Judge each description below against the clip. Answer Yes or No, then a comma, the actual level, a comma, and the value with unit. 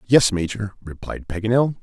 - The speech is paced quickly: No, slow, 130 wpm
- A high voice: No, low, 105 Hz